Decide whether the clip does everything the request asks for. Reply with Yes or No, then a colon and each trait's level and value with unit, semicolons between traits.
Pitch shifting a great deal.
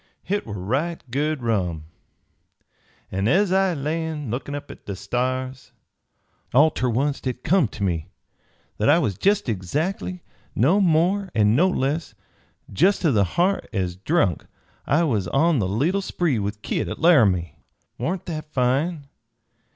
Yes: wide, 8.0 semitones